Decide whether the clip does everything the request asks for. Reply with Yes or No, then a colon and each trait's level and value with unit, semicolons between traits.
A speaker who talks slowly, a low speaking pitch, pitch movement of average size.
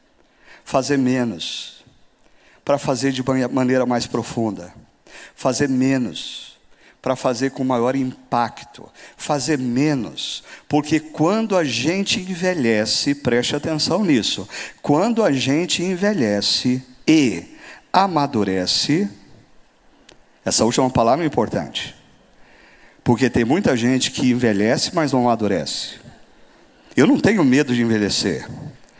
Yes: slow, 105 wpm; low, 130 Hz; average, 3.8 semitones